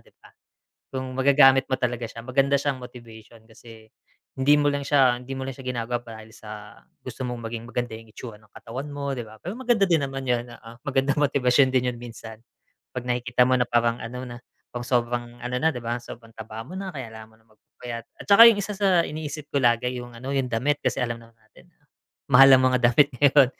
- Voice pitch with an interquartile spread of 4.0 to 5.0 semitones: No, average, 2.9 semitones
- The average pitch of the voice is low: Yes, low, 125 Hz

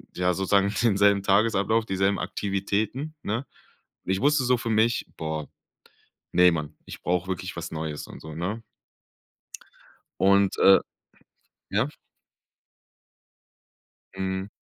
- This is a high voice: No, low, 100 Hz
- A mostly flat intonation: No, average, 3.3 semitones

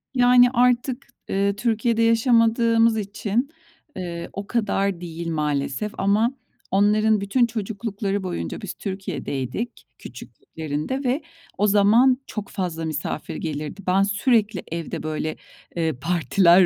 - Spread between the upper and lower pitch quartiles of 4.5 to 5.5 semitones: Yes, average, 5.0 semitones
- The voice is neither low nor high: No, high, 200 Hz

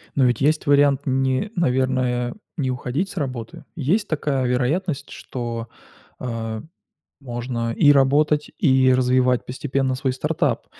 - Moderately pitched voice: No, low, 130 Hz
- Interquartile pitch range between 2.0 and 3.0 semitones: Yes, narrow, 2.5 semitones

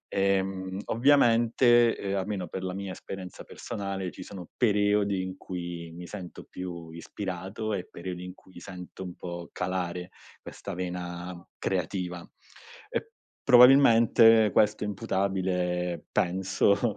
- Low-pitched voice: Yes, very low, 95 Hz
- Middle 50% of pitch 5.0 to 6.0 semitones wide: No, narrow, 2.6 semitones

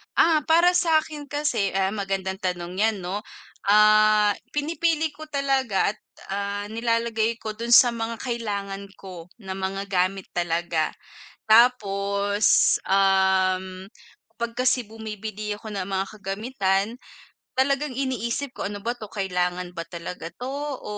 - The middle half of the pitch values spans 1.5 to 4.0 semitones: Yes, average, 3.6 semitones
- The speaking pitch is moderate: No, high, 205 Hz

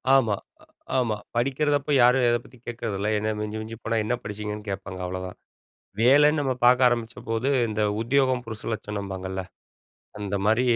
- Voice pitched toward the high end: No, low, 115 Hz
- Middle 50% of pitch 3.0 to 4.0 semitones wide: Yes, average, 3.3 semitones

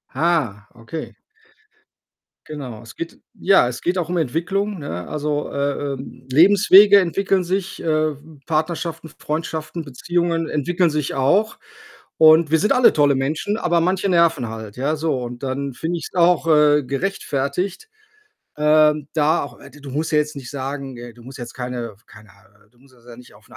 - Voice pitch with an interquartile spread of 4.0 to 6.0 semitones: Yes, average, 4.4 semitones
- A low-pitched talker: No, medium, 150 Hz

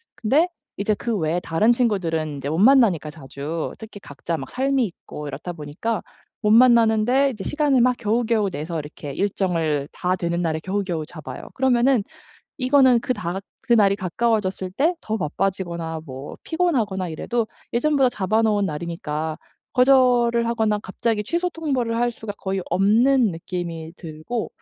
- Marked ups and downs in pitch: Yes, wide, 6.2 semitones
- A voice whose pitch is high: Yes, high, 205 Hz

